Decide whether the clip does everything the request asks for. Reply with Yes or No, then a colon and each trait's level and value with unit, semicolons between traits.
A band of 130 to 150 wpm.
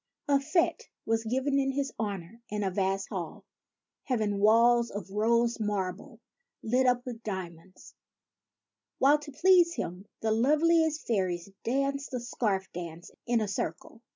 Yes: average, 145 wpm